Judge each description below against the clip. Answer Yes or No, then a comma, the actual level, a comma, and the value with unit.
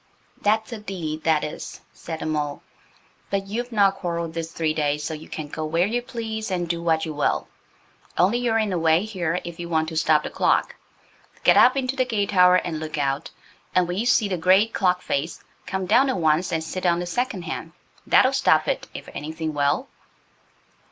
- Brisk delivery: Yes, fast, 210 wpm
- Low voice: No, medium, 175 Hz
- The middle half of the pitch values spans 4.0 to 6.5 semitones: Yes, average, 4.6 semitones